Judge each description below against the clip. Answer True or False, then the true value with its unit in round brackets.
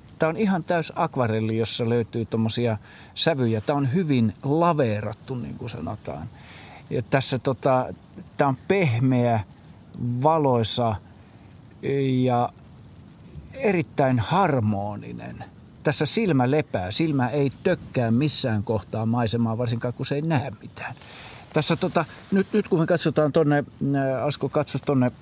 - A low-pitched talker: True (130 Hz)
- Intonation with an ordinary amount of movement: True (4.9 semitones)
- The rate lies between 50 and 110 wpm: False (125 wpm)